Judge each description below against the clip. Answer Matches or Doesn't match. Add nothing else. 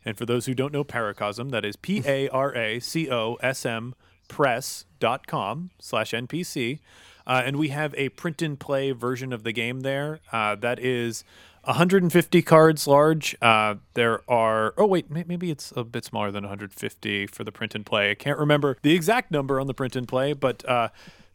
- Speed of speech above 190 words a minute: Matches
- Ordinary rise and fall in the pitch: Matches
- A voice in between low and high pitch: Doesn't match